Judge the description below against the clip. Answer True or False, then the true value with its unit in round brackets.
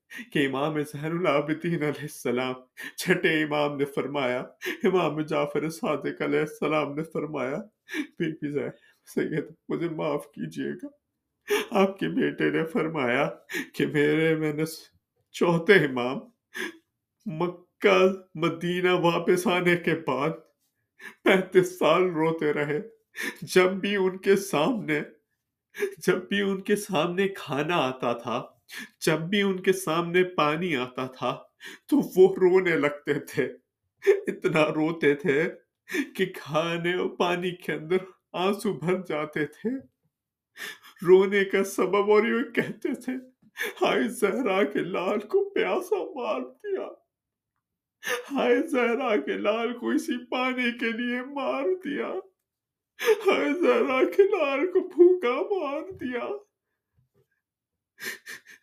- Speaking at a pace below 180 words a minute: True (120 wpm)